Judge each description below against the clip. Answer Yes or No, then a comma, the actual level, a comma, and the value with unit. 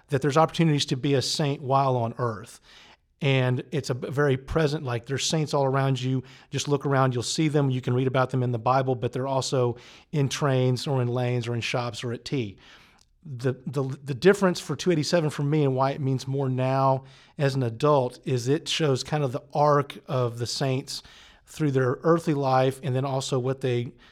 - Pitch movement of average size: No, narrow, 2.2 semitones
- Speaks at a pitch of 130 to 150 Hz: Yes, low, 135 Hz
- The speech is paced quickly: Yes, fast, 210 wpm